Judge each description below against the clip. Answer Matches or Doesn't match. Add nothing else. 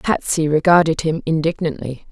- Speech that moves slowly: Matches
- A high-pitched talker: Doesn't match